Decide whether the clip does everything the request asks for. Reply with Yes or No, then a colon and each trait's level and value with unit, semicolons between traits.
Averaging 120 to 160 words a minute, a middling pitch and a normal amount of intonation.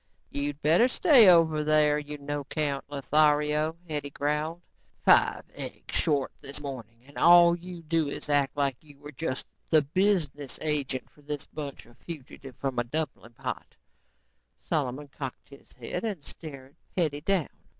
No: average, 155 wpm; medium, 150 Hz; narrow, 2.3 semitones